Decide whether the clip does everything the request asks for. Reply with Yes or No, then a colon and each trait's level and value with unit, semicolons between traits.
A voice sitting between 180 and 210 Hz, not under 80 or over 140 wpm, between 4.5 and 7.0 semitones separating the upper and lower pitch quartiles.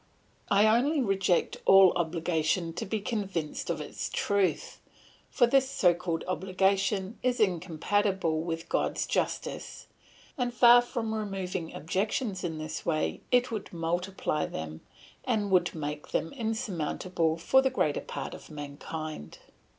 Yes: medium, 185 Hz; slow, 135 wpm; average, 4.9 semitones